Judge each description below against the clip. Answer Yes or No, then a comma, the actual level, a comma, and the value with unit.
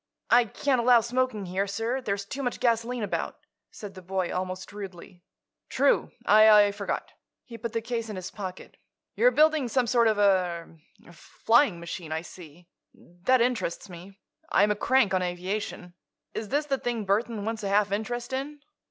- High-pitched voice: Yes, high, 210 Hz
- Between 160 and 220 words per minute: Yes, average, 170 wpm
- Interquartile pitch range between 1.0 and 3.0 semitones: No, average, 4.5 semitones